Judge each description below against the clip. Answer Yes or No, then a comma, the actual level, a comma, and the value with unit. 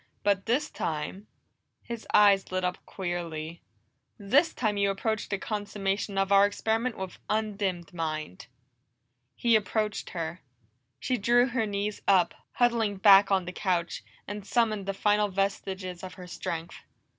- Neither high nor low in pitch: No, high, 200 Hz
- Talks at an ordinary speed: Yes, average, 145 wpm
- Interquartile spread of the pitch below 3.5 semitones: Yes, average, 2.7 semitones